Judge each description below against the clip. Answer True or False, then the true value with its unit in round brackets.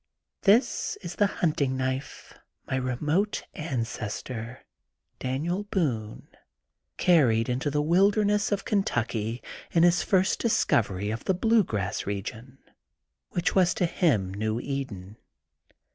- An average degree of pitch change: False (8.2 semitones)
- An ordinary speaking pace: False (125 wpm)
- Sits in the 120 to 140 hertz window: True (135 Hz)